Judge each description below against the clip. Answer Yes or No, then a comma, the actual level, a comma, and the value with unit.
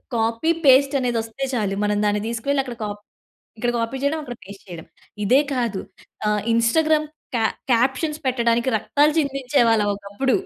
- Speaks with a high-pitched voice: Yes, high, 240 Hz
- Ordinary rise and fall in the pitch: Yes, average, 3.7 semitones